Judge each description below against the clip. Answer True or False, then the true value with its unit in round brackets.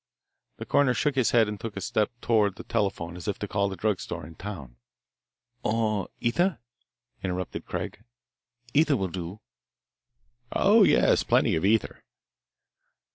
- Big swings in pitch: False (3.9 semitones)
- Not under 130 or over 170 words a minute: True (150 wpm)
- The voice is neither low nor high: False (105 Hz)